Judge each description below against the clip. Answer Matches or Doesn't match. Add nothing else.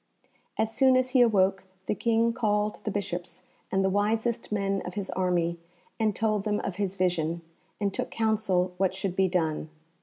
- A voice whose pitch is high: Matches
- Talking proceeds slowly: Doesn't match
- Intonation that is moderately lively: Matches